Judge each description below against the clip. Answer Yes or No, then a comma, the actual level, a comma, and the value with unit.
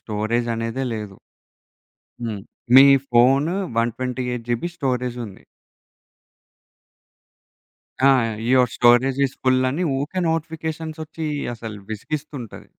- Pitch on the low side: Yes, low, 125 Hz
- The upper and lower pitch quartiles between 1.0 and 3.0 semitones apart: No, average, 3.5 semitones